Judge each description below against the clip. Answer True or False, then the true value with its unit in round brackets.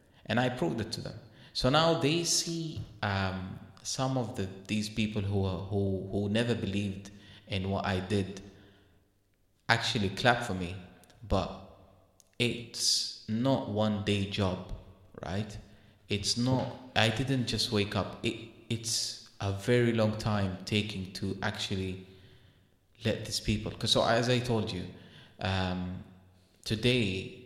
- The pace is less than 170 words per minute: True (140 wpm)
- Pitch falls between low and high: False (105 Hz)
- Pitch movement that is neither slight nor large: True (3.4 semitones)